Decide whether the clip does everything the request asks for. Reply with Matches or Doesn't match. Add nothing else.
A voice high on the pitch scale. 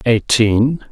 Doesn't match